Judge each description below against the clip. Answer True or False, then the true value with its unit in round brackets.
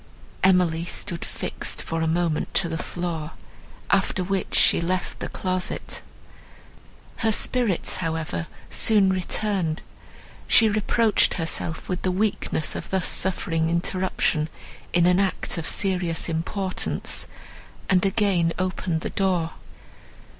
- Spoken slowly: True (120 wpm)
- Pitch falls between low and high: True (180 Hz)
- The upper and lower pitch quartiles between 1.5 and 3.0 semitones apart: True (2.6 semitones)